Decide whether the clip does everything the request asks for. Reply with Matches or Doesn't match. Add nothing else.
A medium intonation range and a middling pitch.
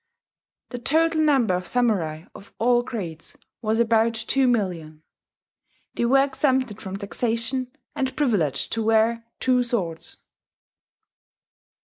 Doesn't match